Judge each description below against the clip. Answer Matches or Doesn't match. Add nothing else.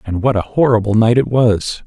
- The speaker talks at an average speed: Doesn't match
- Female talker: Doesn't match